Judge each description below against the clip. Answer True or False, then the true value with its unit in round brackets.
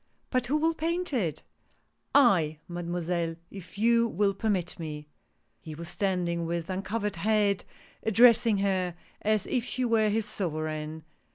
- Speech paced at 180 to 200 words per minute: False (160 wpm)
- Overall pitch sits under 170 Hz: False (195 Hz)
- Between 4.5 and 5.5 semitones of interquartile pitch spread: True (5.0 semitones)